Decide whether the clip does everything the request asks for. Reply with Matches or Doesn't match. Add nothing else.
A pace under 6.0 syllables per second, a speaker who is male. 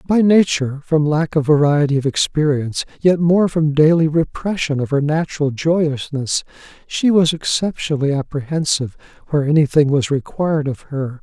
Matches